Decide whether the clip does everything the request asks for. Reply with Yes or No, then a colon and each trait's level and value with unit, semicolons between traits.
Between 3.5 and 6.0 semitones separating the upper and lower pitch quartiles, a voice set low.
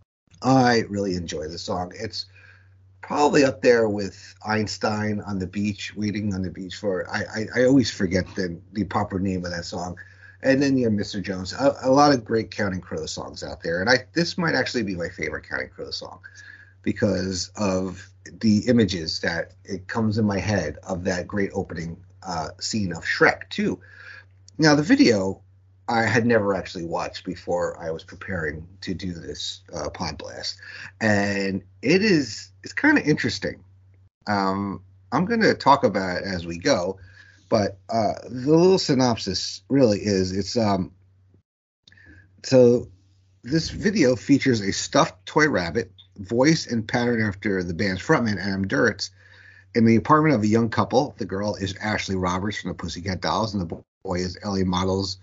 No: average, 3.1 semitones; low, 100 Hz